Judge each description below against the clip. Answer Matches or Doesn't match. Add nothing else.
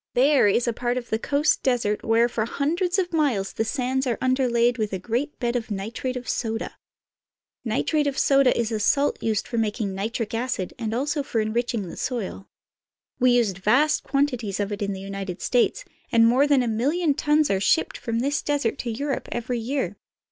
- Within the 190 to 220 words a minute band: Matches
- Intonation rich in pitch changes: Doesn't match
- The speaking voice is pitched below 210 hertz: Doesn't match